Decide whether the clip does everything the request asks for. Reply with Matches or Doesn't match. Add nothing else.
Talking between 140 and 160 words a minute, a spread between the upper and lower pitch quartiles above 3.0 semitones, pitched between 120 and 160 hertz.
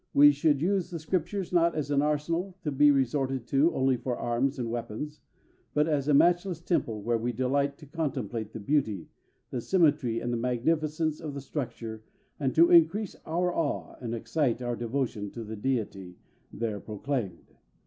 Doesn't match